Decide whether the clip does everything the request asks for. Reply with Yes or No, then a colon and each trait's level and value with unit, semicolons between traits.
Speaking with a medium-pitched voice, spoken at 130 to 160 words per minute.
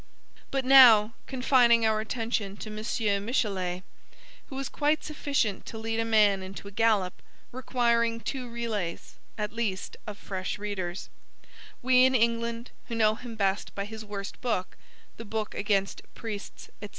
No: high, 220 Hz; average, 150 wpm